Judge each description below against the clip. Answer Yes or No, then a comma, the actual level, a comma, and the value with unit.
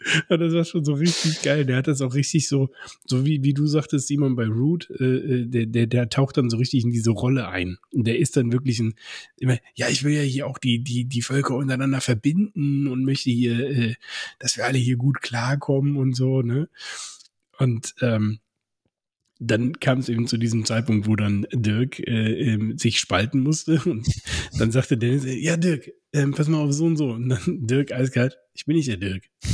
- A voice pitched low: Yes, low, 130 Hz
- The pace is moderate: No, fast, 210 wpm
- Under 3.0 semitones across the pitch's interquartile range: No, average, 3.3 semitones